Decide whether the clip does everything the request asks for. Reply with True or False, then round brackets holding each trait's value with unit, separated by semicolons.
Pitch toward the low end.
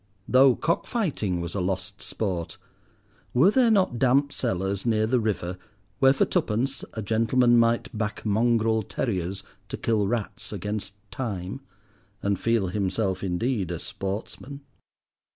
True (110 Hz)